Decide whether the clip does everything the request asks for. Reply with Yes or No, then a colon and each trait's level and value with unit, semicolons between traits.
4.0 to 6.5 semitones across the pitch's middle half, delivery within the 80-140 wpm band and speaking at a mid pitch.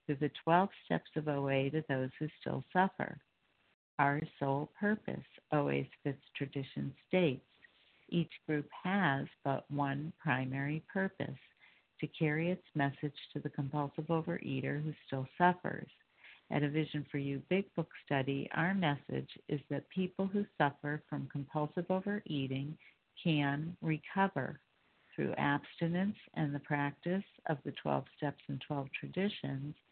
No: average, 3.3 semitones; slow, 135 wpm; medium, 150 Hz